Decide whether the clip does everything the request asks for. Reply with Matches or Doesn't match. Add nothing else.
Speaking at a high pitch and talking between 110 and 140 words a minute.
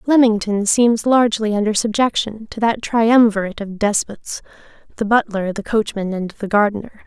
Matches